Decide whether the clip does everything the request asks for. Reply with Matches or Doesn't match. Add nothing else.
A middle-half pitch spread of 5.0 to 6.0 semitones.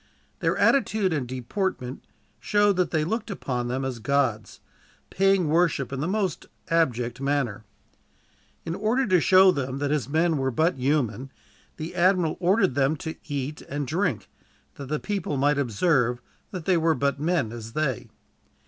Matches